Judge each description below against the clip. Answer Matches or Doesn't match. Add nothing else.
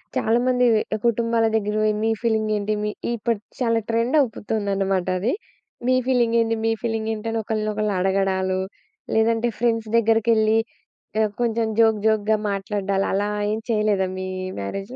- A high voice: Matches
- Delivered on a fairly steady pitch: Matches